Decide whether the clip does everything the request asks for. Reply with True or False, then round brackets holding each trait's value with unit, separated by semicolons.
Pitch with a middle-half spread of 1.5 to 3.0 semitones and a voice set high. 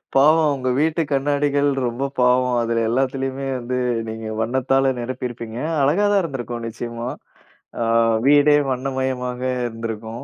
False (2.6 semitones; 130 Hz)